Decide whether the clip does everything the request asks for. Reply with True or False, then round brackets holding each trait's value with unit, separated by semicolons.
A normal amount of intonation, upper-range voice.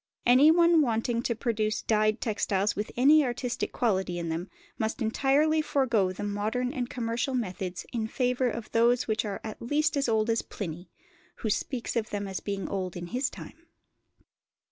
True (3.6 semitones; 230 Hz)